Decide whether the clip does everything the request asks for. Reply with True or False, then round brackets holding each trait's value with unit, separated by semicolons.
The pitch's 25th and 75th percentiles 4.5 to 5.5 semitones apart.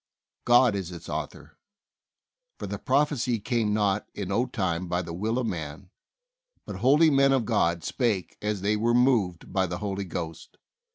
True (5.1 semitones)